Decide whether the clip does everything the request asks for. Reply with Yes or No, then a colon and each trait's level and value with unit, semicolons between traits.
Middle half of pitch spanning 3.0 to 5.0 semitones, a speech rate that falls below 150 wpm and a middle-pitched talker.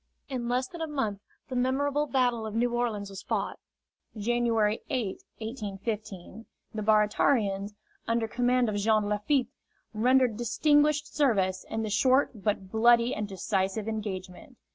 No: average, 3.3 semitones; average, 140 wpm; high, 225 Hz